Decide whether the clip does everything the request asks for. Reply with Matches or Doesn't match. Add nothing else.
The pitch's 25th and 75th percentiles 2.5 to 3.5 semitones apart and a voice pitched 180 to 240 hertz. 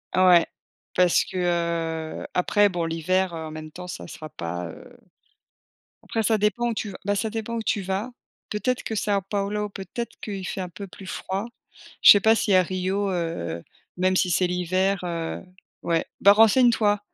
Matches